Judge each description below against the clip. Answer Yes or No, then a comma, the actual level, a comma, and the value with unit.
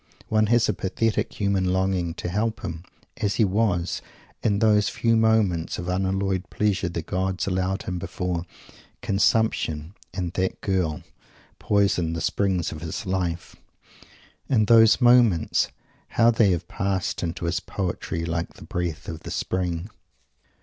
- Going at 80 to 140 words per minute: No, average, 150 wpm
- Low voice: Yes, very low, 95 Hz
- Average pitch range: Yes, average, 3.2 semitones